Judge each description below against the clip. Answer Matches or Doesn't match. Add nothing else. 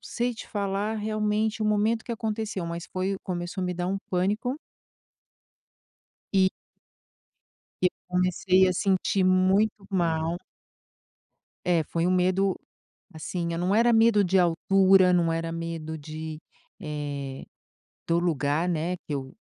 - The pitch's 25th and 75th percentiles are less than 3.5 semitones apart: Matches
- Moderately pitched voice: Matches